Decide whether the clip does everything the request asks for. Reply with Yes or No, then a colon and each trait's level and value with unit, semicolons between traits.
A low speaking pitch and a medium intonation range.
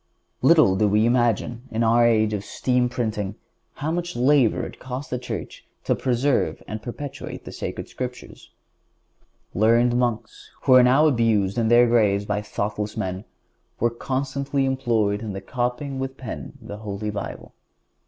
Yes: low, 120 Hz; average, 3.3 semitones